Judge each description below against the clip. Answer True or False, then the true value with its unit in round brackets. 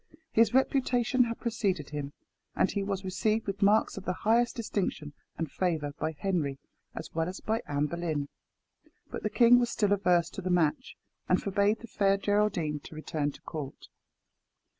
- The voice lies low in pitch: False (190 Hz)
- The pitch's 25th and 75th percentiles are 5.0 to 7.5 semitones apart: True (5.5 semitones)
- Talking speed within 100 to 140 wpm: False (175 wpm)